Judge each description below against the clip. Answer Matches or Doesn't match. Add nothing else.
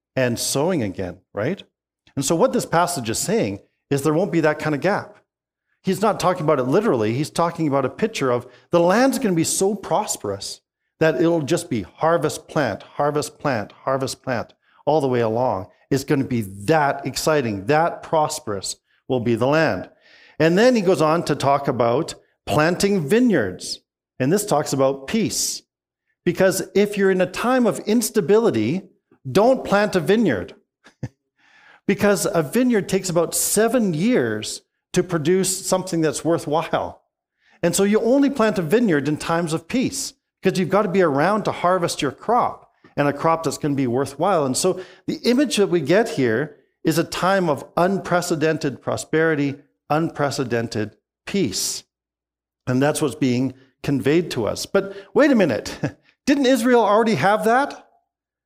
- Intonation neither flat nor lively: Doesn't match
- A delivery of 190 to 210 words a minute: Doesn't match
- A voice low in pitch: Doesn't match